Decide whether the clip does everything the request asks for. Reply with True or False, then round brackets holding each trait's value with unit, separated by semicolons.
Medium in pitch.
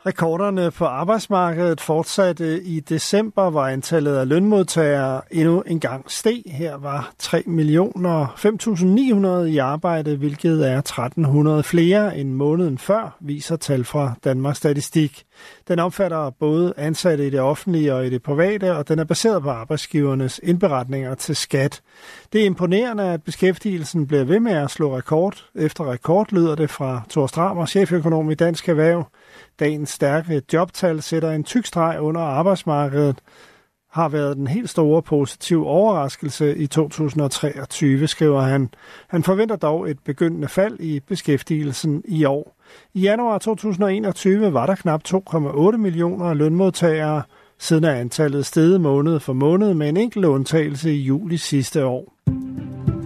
True (160 Hz)